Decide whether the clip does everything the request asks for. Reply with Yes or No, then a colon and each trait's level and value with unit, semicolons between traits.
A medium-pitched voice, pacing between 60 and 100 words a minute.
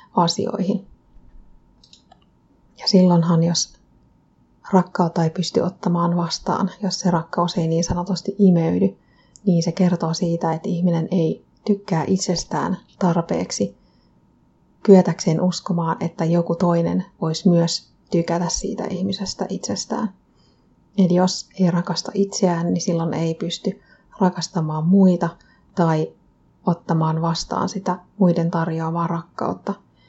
No: medium, 175 Hz; average, 110 wpm